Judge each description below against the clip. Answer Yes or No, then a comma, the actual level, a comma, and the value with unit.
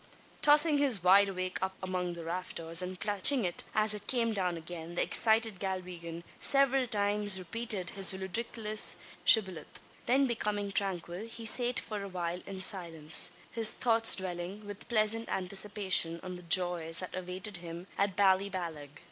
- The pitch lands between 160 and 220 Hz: Yes, high, 190 Hz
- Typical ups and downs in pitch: Yes, average, 3.3 semitones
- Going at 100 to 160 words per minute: Yes, average, 150 wpm